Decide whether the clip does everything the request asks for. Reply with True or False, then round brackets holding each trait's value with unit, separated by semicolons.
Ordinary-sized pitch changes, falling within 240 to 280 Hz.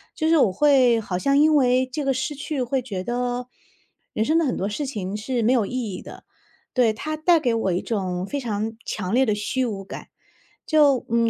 True (4.6 semitones; 245 Hz)